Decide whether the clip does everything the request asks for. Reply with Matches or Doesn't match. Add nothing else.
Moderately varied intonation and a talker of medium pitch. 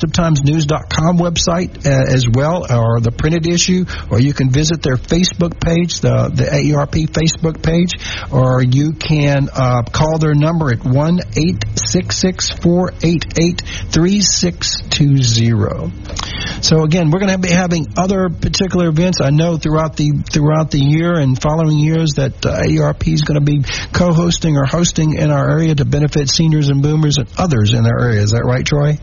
Matches